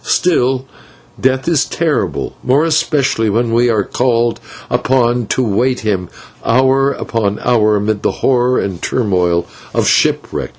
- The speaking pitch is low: Yes, low, 120 Hz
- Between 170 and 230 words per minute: No, average, 140 wpm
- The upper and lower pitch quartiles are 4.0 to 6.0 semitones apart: No, average, 3.6 semitones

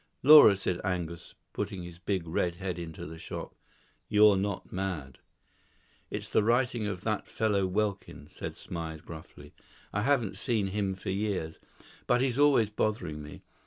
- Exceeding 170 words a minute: No, average, 155 wpm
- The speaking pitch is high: No, very low, 95 Hz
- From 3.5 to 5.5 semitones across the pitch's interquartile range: Yes, average, 4.0 semitones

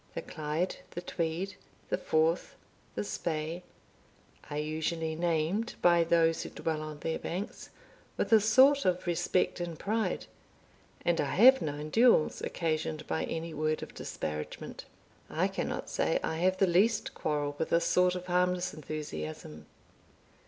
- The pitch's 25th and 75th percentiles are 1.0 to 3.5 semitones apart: Yes, average, 2.9 semitones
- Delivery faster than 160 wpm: No, average, 145 wpm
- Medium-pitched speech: Yes, medium, 165 Hz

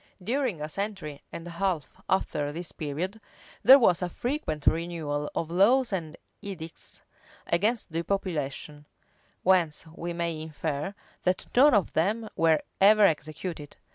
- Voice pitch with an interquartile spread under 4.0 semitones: No, average, 4.3 semitones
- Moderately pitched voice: Yes, medium, 170 Hz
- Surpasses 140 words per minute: No, slow, 135 wpm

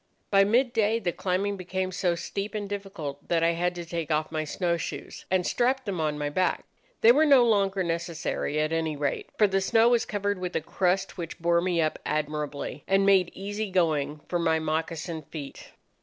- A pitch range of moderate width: Yes, average, 3.8 semitones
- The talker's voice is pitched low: No, medium, 180 Hz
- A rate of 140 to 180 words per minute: No, average, 200 wpm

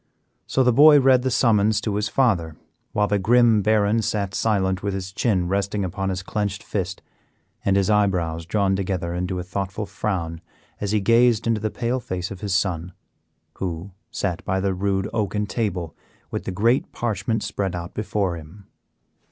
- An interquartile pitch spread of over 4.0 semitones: No, average, 2.7 semitones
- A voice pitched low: Yes, low, 100 Hz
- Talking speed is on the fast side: No, average, 175 wpm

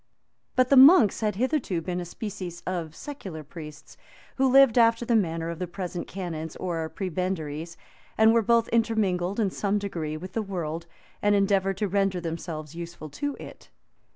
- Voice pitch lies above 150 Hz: Yes, medium, 185 Hz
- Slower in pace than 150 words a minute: No, average, 170 wpm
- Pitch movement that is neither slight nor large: Yes, average, 4.7 semitones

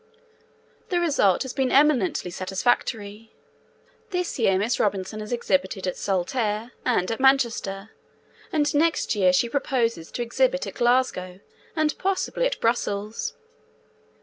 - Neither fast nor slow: No, slow, 125 wpm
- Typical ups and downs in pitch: No, wide, 5.7 semitones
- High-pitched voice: Yes, high, 235 Hz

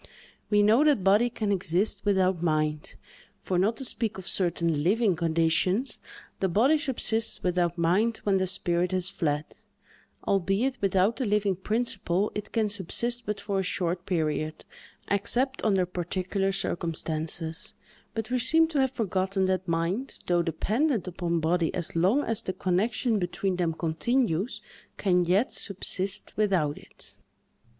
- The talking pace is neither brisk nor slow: Yes, average, 145 wpm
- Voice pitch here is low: No, high, 190 Hz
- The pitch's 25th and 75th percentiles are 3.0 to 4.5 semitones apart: Yes, average, 4.1 semitones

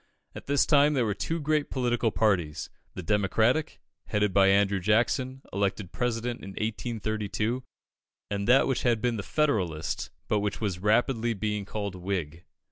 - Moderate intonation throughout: Yes, average, 3.7 semitones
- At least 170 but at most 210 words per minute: No, average, 155 wpm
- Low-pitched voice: Yes, low, 110 Hz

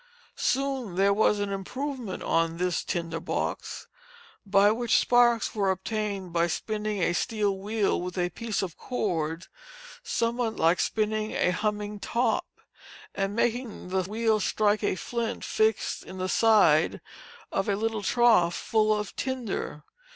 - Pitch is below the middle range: No, high, 210 Hz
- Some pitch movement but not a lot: Yes, average, 3.3 semitones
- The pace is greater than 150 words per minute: No, average, 145 wpm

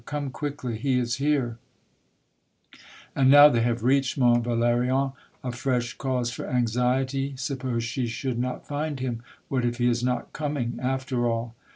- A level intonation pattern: Yes, narrow, 2.1 semitones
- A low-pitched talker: Yes, low, 125 Hz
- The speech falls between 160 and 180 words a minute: Yes, average, 170 wpm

